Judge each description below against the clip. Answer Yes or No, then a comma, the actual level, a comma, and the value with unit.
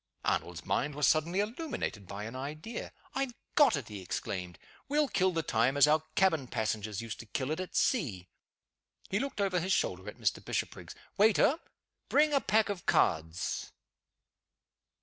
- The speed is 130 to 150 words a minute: No, average, 170 wpm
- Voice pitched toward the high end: No, medium, 155 Hz